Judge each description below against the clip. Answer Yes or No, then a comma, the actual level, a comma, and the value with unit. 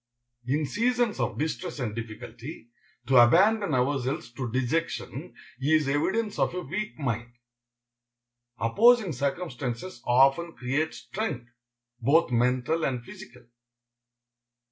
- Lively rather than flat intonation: Yes, wide, 5.8 semitones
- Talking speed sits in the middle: No, slow, 105 wpm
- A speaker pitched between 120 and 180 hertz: Yes, medium, 140 Hz